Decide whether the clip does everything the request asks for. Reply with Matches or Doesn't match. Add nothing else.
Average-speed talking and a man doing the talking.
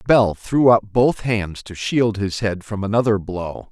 Matches